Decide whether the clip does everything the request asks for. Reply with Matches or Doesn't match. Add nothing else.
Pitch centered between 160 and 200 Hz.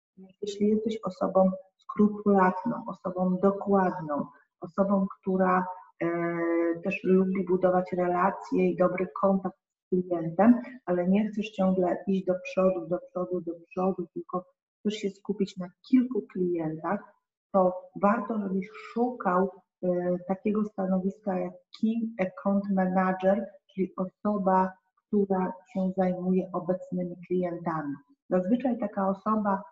Matches